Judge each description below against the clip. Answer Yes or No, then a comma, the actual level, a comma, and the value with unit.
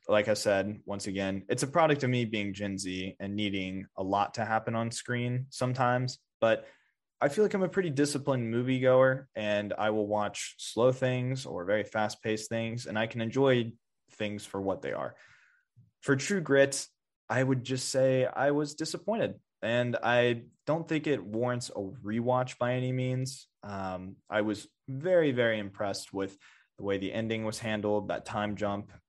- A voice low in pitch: Yes, low, 115 Hz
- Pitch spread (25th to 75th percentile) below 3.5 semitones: No, average, 4.2 semitones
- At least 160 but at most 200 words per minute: Yes, average, 180 wpm